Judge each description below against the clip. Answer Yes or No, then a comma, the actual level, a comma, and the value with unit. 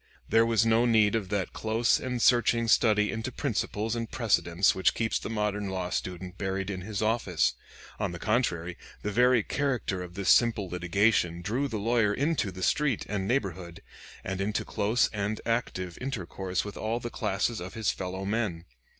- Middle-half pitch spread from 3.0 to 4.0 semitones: Yes, average, 3.6 semitones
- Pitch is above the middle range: No, low, 105 Hz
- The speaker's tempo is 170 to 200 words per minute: Yes, average, 175 wpm